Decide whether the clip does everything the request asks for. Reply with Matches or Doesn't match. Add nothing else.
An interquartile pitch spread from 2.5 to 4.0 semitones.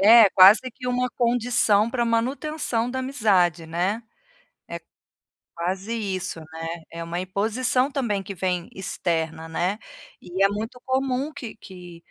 Doesn't match